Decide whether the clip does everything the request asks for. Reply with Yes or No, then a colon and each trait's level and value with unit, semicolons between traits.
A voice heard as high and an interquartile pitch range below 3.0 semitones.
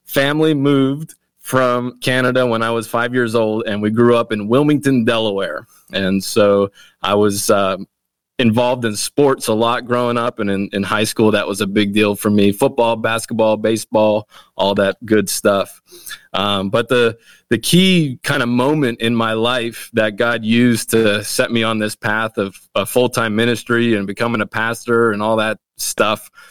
No: low, 115 Hz; narrow, 2.5 semitones